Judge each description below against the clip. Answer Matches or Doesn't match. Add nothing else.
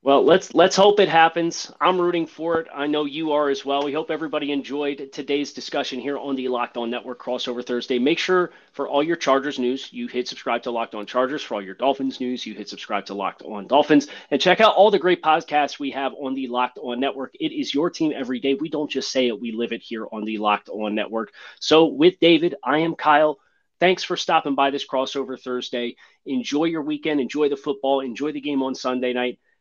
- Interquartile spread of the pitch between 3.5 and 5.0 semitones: Matches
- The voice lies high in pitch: Doesn't match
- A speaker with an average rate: Doesn't match